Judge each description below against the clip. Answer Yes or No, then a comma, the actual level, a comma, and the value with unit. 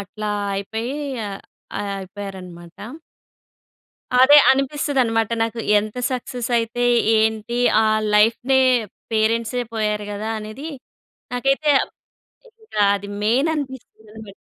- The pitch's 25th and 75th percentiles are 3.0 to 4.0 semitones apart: Yes, average, 3.3 semitones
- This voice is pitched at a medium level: No, high, 225 Hz